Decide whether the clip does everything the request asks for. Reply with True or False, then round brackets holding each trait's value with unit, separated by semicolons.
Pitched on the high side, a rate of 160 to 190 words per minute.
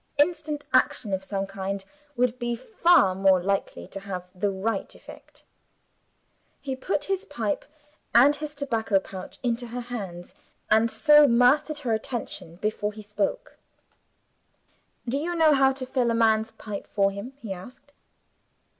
False (230 Hz; 150 wpm)